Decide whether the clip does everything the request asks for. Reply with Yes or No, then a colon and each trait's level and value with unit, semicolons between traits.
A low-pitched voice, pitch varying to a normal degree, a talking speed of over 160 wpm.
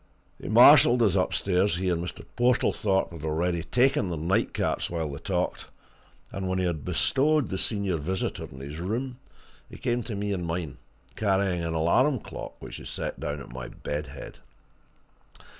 Yes: very low, 90 Hz; average, 4.0 semitones; average, 175 wpm